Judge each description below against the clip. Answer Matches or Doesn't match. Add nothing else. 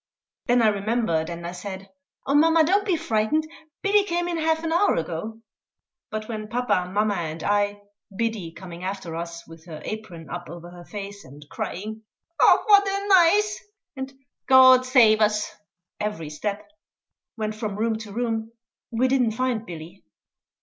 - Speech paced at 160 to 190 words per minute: Matches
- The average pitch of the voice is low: Doesn't match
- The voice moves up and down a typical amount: Doesn't match